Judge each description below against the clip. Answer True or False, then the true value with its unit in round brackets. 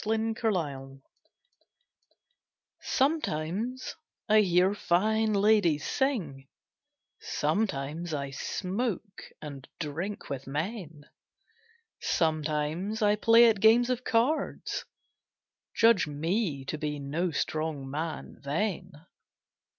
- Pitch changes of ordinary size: False (6.6 semitones)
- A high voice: False (180 Hz)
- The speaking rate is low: True (90 wpm)